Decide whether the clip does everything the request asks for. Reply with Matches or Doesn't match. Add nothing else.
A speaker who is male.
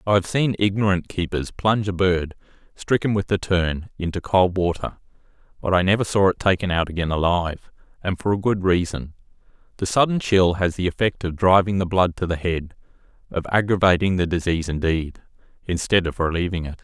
Matches